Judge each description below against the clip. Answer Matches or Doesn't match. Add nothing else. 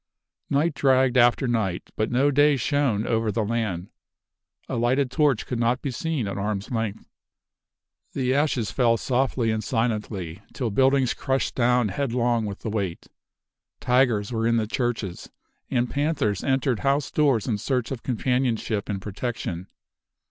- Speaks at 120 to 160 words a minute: Matches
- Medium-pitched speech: Doesn't match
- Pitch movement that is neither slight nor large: Matches